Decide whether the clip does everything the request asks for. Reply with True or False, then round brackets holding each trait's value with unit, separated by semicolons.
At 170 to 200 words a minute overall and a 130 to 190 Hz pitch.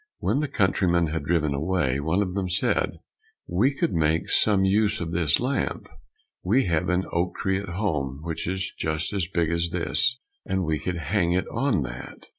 False (190 wpm; 90 Hz)